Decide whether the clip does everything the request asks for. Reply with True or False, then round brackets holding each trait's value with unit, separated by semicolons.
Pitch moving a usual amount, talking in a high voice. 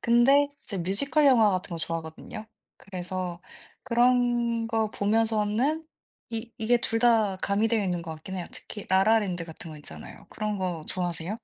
True (4.3 semitones; 210 Hz)